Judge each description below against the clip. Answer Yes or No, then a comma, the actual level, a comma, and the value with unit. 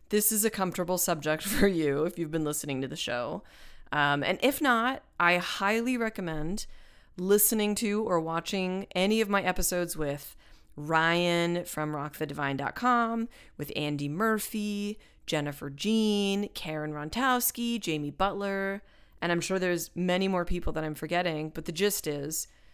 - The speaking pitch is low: No, medium, 180 Hz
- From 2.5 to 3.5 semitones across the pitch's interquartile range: No, average, 5.1 semitones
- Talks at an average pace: Yes, average, 150 wpm